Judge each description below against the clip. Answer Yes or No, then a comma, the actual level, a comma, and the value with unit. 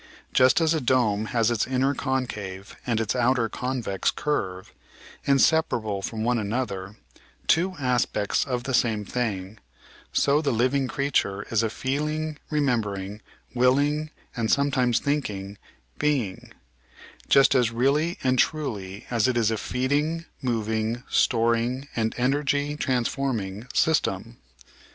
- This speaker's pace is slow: Yes, slow, 130 wpm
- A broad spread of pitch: No, average, 4.1 semitones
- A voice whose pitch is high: No, low, 125 Hz